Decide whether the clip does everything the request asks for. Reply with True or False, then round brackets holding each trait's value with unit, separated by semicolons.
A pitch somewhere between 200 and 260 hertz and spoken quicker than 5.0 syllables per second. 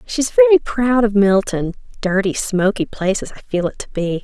True (210 Hz; 5.2 syllables/s)